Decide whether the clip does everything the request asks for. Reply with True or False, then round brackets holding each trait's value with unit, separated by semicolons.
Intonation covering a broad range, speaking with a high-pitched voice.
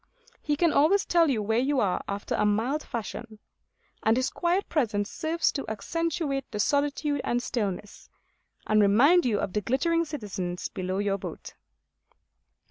True (6.6 semitones; 250 Hz)